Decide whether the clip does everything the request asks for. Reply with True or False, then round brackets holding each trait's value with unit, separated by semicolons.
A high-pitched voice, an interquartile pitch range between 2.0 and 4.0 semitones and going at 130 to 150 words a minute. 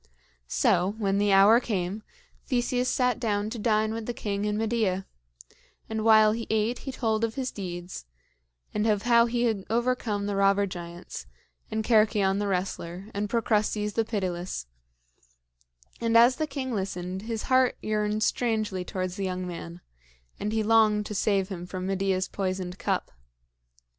False (210 Hz; 2.9 semitones; 160 wpm)